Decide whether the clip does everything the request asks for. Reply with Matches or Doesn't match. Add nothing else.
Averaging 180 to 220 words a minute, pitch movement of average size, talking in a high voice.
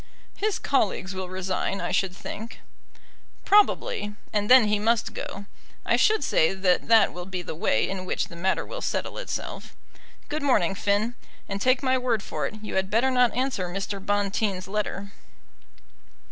Doesn't match